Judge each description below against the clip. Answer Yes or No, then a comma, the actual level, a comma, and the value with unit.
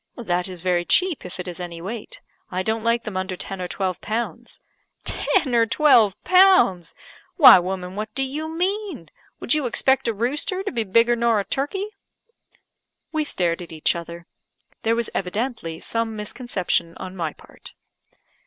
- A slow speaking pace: No, average, 170 wpm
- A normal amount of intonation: No, wide, 6.6 semitones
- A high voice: Yes, high, 220 Hz